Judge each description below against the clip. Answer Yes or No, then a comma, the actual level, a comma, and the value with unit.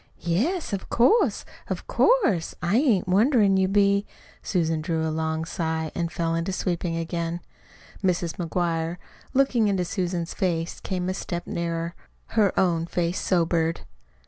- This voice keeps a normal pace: Yes, average, 145 wpm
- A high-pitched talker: No, medium, 175 Hz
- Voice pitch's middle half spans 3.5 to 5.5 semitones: No, average, 2.9 semitones